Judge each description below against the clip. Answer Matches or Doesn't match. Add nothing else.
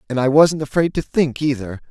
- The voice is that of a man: Matches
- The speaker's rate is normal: Doesn't match